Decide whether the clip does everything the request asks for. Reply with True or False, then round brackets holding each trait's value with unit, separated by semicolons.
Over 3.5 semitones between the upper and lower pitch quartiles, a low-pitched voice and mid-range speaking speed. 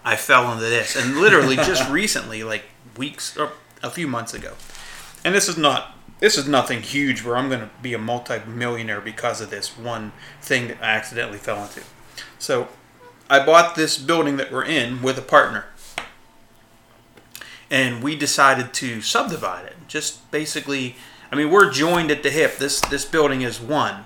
True (3.9 semitones; 125 Hz; 175 wpm)